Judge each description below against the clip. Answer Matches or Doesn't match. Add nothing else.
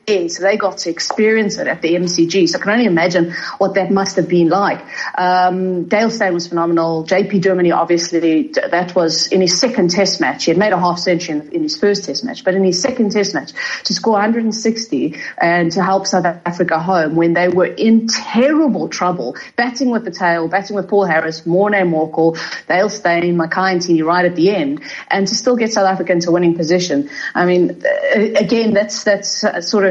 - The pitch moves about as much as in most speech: Matches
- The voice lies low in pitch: Doesn't match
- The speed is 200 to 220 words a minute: Matches